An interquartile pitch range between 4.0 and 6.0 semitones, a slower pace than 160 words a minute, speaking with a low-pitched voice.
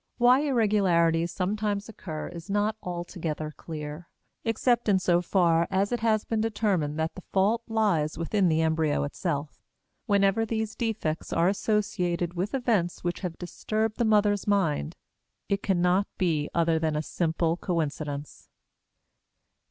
No: average, 4.4 semitones; average, 140 wpm; medium, 180 Hz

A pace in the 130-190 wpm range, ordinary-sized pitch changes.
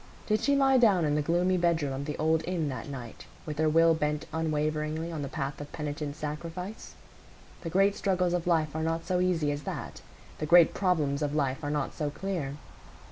No: fast, 205 wpm; average, 3.1 semitones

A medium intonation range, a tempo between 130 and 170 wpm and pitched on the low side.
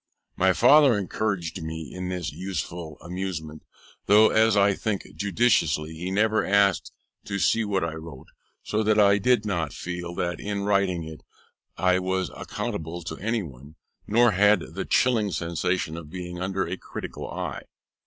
Yes: average, 3.6 semitones; average, 160 wpm; very low, 95 Hz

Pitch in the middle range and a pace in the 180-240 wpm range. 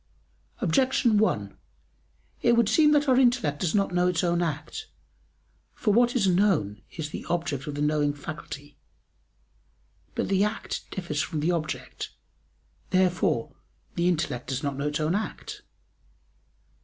No: medium, 175 Hz; average, 145 wpm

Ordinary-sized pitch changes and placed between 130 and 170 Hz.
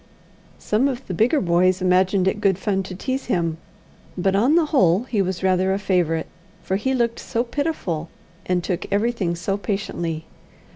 No: average, 4.4 semitones; high, 195 Hz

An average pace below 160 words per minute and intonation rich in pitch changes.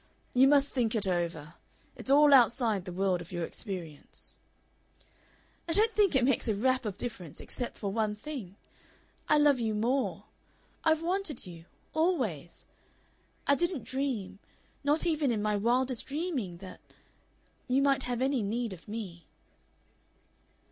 Yes: average, 150 wpm; wide, 6.1 semitones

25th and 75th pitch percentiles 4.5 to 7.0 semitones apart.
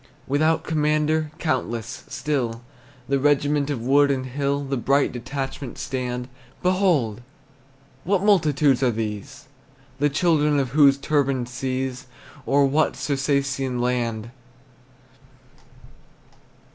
No: average, 2.9 semitones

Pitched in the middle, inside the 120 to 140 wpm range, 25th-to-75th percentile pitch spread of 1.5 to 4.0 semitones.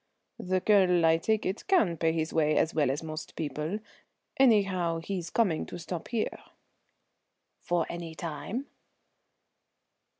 Yes: medium, 170 Hz; slow, 135 wpm; average, 3.4 semitones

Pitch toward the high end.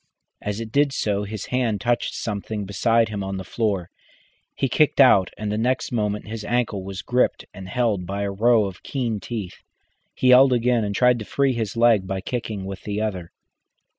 No: low, 110 Hz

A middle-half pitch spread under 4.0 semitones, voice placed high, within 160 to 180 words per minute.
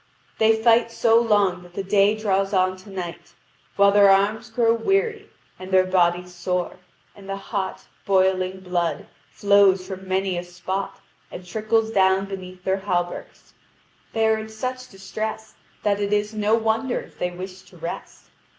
Yes: average, 2.8 semitones; high, 195 Hz; average, 165 wpm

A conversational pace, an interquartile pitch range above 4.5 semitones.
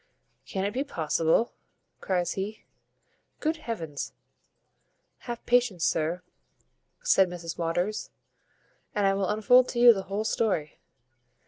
No: slow, 120 wpm; average, 5.0 semitones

